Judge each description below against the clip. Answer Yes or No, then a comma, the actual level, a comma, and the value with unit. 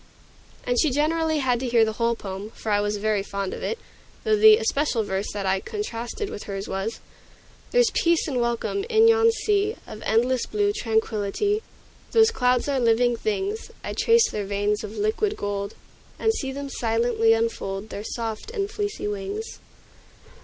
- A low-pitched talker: No, high, 240 Hz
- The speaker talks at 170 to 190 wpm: Yes, average, 175 wpm